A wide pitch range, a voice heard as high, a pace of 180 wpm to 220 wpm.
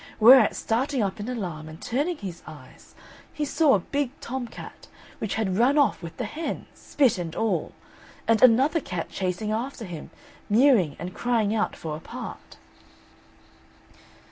No: wide, 6.4 semitones; high, 220 Hz; average, 160 wpm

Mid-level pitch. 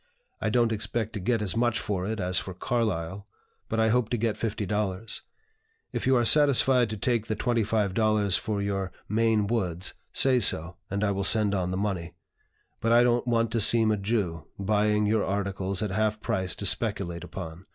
No: low, 105 Hz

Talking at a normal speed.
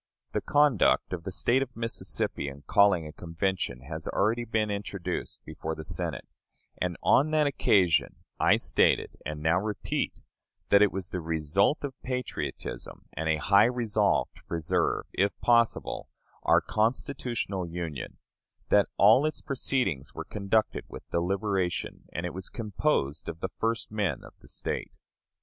Yes: average, 150 wpm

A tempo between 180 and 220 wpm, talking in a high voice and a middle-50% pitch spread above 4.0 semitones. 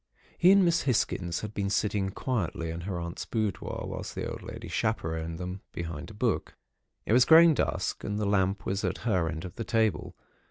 No: average, 200 wpm; low, 100 Hz; average, 4.5 semitones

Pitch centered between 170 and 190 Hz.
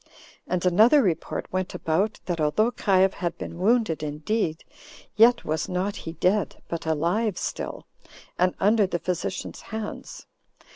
Yes: medium, 185 Hz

